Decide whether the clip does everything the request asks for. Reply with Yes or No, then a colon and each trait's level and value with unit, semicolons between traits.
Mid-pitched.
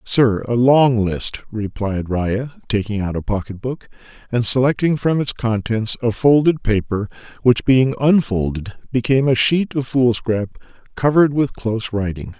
No: low, 120 Hz